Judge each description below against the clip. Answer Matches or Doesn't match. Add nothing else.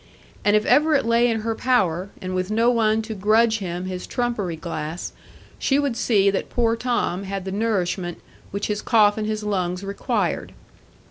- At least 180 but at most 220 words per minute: Matches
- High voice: Matches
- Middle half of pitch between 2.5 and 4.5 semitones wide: Matches